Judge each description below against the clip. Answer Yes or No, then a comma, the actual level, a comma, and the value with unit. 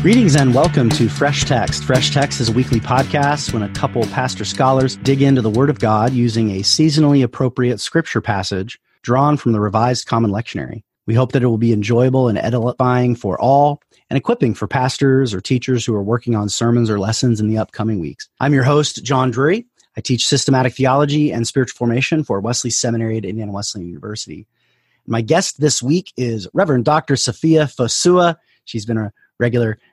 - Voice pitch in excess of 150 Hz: No, low, 125 Hz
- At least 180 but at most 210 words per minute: Yes, average, 195 wpm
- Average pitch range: Yes, average, 3.6 semitones